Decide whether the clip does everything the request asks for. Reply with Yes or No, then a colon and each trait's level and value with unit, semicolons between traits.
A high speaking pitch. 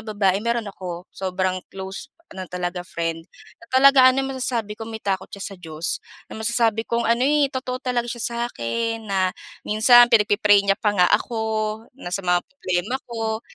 Yes: high, 215 Hz